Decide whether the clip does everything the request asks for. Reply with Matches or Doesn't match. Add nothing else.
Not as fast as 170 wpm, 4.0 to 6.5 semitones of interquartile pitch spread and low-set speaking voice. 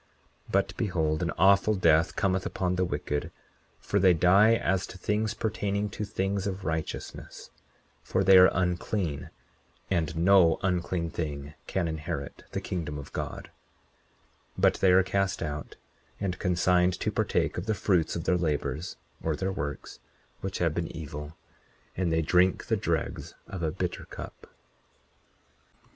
Doesn't match